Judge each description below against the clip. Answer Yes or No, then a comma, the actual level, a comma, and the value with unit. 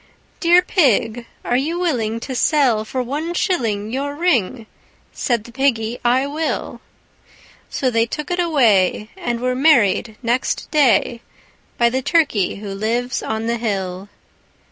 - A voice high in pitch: Yes, high, 245 Hz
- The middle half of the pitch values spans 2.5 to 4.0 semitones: No, average, 4.5 semitones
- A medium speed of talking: Yes, average, 145 wpm